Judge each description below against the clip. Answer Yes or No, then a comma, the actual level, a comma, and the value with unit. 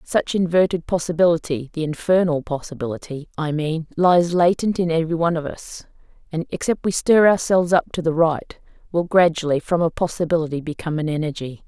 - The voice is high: No, medium, 165 Hz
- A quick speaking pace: No, average, 165 wpm